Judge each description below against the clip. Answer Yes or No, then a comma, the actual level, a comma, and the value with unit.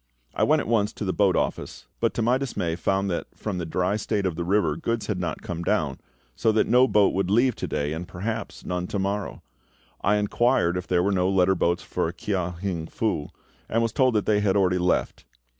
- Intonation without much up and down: No, average, 3.3 semitones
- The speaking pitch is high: No, very low, 95 Hz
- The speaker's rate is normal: No, fast, 225 wpm